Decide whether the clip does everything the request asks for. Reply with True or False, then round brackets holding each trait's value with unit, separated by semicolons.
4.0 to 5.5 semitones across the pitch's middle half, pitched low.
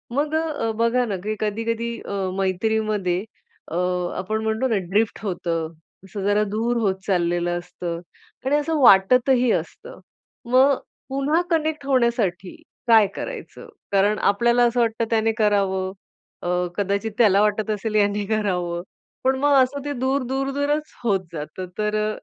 False (4.5 semitones; 220 Hz)